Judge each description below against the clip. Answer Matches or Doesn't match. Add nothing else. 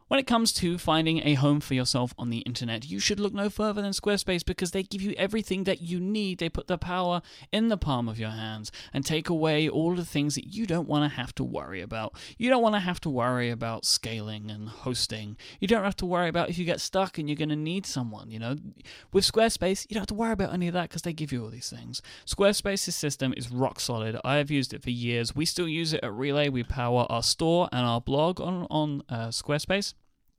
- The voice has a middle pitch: Matches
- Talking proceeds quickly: Matches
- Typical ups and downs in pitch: Doesn't match